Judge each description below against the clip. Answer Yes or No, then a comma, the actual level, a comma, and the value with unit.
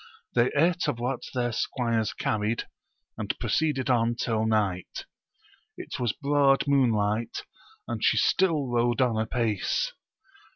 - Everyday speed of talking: No, slow, 130 wpm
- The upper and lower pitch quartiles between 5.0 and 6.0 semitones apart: No, average, 3.5 semitones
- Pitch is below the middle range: Yes, low, 120 Hz